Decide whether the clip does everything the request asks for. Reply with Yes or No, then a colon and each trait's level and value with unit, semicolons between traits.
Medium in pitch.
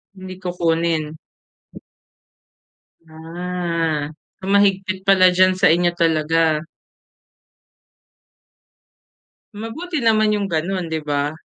Yes: medium, 180 Hz